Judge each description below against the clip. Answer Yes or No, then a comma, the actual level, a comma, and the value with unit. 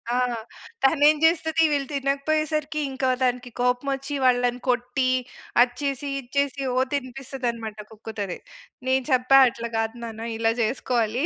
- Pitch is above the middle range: Yes, very high, 255 Hz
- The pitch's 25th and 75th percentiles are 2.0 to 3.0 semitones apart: Yes, narrow, 2.5 semitones